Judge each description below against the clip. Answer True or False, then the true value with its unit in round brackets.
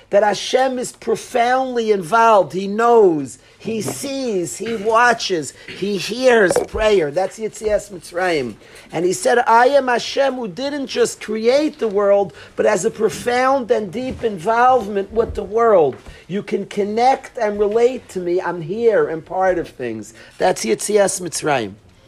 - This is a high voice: True (215 Hz)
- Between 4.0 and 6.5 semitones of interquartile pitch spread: True (4.3 semitones)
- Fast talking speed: False (150 wpm)